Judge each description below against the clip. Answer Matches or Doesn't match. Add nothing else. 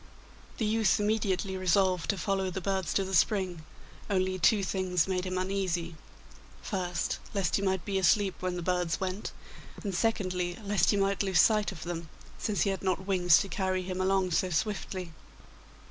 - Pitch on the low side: Doesn't match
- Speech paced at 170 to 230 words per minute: Matches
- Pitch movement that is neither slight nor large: Doesn't match